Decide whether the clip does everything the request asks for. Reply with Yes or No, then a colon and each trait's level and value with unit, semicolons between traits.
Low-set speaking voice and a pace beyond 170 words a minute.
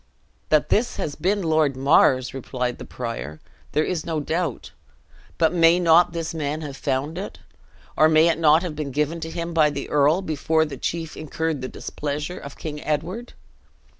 No: medium, 155 Hz; average, 180 wpm